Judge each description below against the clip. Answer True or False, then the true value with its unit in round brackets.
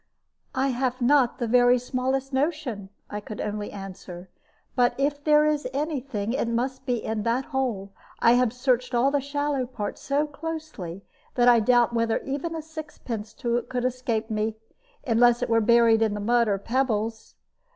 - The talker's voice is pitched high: True (245 Hz)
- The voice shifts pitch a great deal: False (3.4 semitones)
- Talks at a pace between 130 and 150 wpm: False (170 wpm)